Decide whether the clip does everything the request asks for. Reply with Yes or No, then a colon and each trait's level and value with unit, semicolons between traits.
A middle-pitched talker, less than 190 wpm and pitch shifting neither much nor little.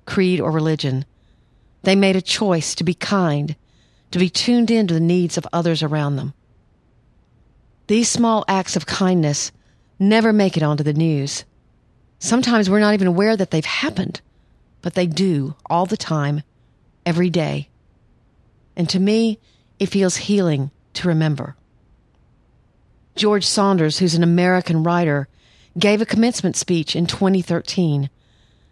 Yes: medium, 175 Hz; average, 140 wpm; average, 4.6 semitones